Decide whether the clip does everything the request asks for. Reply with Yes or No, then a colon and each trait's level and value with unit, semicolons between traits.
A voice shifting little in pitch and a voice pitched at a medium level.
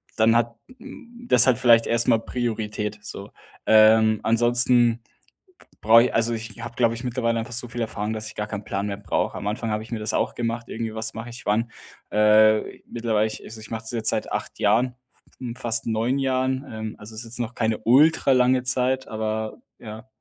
No: narrow, 1.8 semitones; low, 115 Hz